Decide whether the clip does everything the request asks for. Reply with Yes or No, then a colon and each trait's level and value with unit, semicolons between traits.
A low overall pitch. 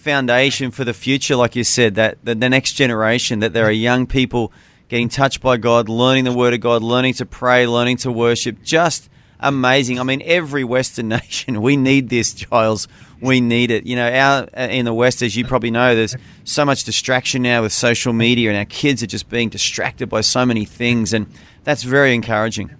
Yes: low, 125 Hz